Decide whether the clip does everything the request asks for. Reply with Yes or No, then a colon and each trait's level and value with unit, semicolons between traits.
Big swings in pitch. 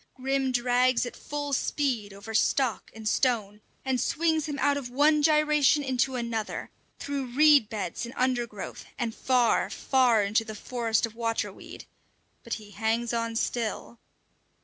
No: average, 3.3 semitones